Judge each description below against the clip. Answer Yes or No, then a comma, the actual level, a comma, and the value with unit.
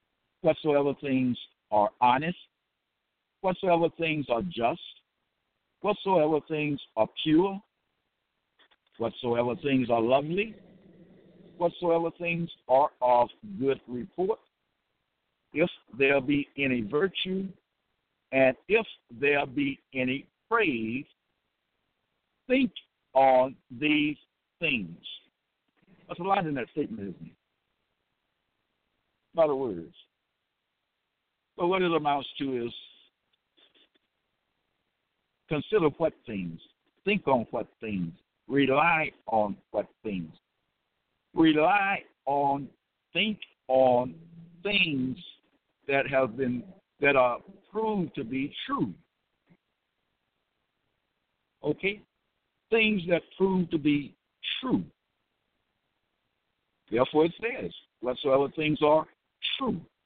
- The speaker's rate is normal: No, slow, 90 wpm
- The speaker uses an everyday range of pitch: No, wide, 5.7 semitones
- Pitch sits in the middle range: Yes, medium, 150 Hz